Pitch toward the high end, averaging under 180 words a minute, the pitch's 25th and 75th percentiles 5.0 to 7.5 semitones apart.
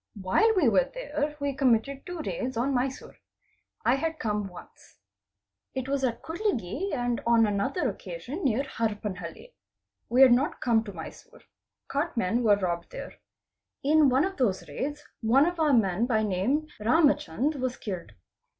Yes: very high, 255 Hz; average, 160 wpm; wide, 5.5 semitones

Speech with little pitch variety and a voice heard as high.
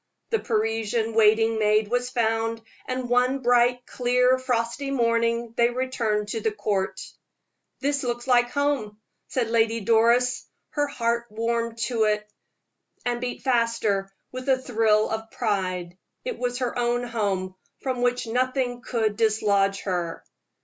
Yes: narrow, 2.3 semitones; high, 230 Hz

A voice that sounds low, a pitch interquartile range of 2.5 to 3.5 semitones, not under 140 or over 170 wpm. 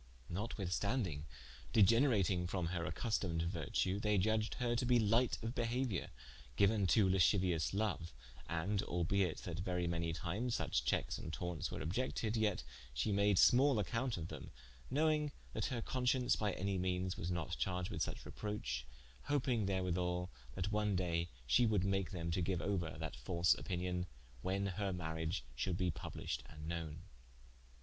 No: very low, 95 Hz; average, 4.0 semitones; average, 155 wpm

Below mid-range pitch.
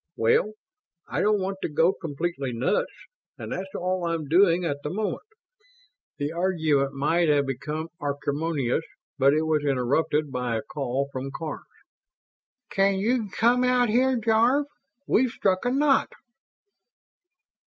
No: medium, 165 Hz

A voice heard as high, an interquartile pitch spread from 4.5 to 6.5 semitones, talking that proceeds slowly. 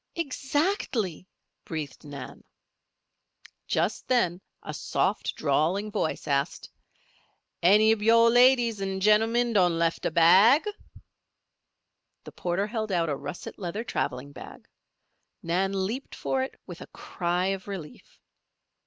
Yes: high, 195 Hz; average, 5.3 semitones; slow, 120 wpm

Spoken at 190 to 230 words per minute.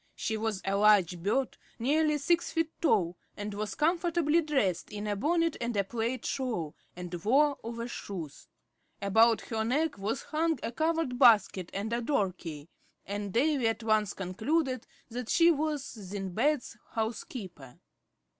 No: average, 150 wpm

